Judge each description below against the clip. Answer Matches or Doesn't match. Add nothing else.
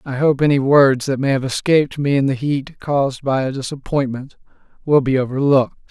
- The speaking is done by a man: Matches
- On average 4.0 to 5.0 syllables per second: Doesn't match